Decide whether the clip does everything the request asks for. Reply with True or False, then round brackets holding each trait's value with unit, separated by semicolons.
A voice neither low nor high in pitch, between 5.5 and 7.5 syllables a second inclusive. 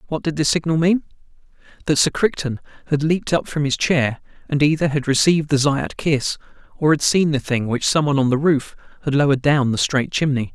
True (145 Hz; 5.8 syllables/s)